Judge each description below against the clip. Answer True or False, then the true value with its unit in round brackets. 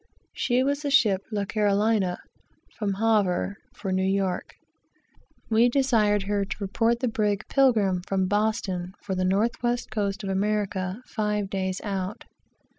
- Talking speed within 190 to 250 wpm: False (145 wpm)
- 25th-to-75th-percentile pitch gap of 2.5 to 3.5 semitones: True (2.8 semitones)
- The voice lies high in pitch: True (205 Hz)